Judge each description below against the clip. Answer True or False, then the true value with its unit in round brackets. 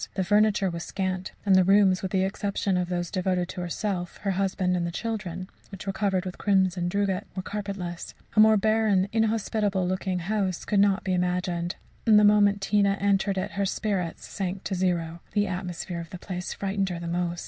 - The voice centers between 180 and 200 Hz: True (190 Hz)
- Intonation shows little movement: True (2.1 semitones)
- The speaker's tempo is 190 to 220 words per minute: True (200 wpm)